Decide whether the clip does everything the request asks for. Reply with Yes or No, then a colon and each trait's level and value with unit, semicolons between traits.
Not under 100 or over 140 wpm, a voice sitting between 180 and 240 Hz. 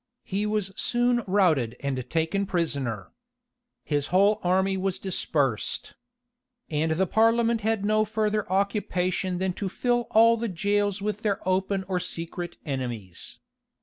Yes: slow, 135 wpm; high, 190 Hz